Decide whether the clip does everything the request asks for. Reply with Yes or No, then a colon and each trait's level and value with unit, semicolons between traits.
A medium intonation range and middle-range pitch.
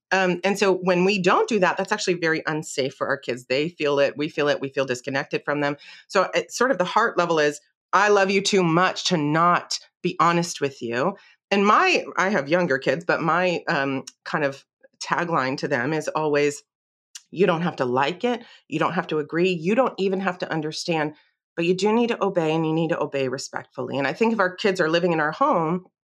Yes: average, 4.6 semitones; medium, 170 Hz